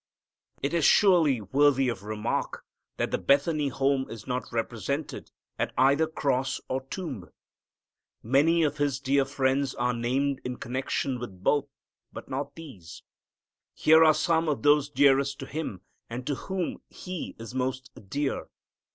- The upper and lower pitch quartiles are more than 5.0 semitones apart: No, average, 2.7 semitones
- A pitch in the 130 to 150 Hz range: Yes, low, 135 Hz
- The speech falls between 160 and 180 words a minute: No, average, 150 wpm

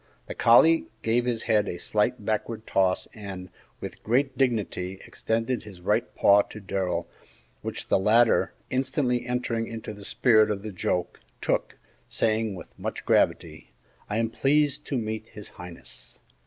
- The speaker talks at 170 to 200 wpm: No, average, 155 wpm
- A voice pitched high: No, low, 110 Hz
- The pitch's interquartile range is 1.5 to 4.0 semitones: Yes, average, 3.3 semitones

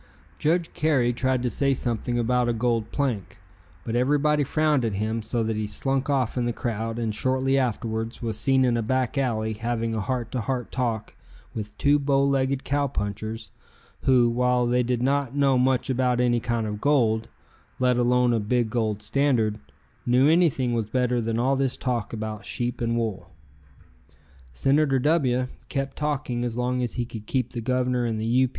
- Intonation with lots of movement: No, average, 2.7 semitones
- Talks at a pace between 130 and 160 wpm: No, average, 185 wpm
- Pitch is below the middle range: Yes, low, 125 Hz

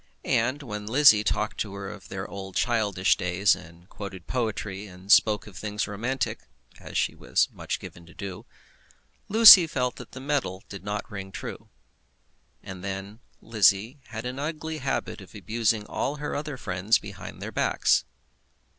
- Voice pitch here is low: Yes, low, 105 Hz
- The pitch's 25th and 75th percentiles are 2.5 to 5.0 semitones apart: Yes, average, 4.5 semitones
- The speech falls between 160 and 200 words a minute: Yes, average, 165 wpm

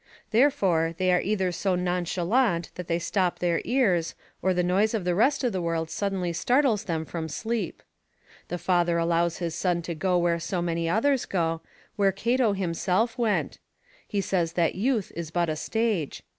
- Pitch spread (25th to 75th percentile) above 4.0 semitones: No, average, 3.7 semitones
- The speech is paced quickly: No, average, 180 wpm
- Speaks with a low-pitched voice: No, medium, 180 Hz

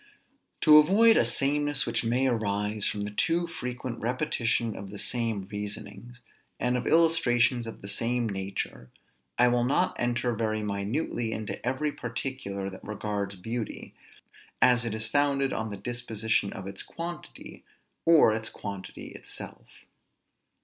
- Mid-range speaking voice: No, low, 115 Hz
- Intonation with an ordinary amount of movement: Yes, average, 3.7 semitones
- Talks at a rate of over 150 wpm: No, average, 145 wpm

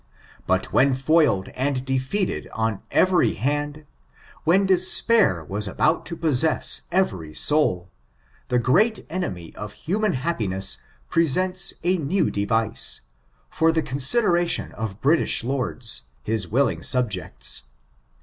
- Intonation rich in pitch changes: Yes, wide, 7.8 semitones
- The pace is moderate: No, slow, 115 wpm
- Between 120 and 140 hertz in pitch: Yes, low, 135 Hz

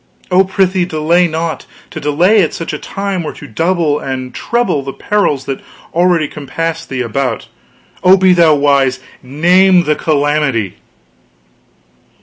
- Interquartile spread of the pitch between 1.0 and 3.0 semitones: No, average, 4.3 semitones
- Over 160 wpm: No, average, 140 wpm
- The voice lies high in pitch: No, medium, 160 Hz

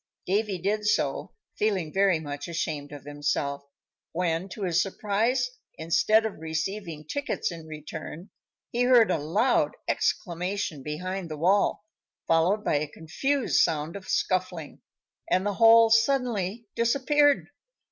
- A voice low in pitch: No, medium, 185 Hz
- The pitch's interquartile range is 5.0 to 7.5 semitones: Yes, average, 5.3 semitones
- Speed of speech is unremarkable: No, slow, 130 wpm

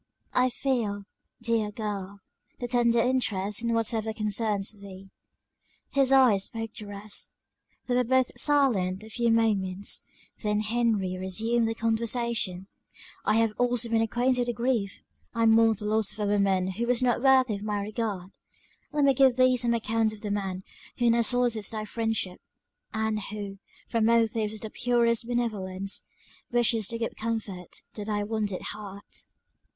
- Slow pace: No, average, 160 wpm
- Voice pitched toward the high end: Yes, high, 225 Hz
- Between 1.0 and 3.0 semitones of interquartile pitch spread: Yes, narrow, 2.6 semitones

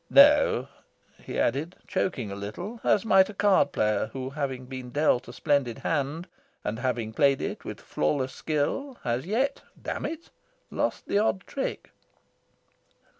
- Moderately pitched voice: Yes, medium, 145 Hz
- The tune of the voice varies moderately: No, wide, 8.0 semitones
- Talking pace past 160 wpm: No, average, 150 wpm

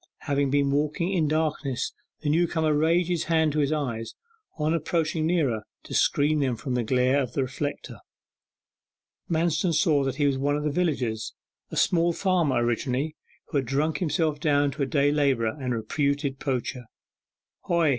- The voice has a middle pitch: Yes, medium, 145 Hz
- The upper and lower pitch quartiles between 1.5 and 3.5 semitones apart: Yes, average, 3.0 semitones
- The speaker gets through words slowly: No, average, 170 wpm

